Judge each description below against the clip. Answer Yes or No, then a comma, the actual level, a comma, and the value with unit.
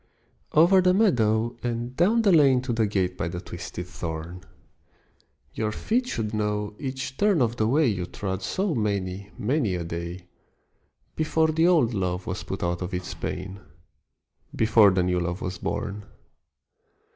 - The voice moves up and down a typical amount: No, wide, 7.1 semitones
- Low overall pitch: Yes, low, 105 Hz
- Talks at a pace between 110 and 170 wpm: Yes, average, 160 wpm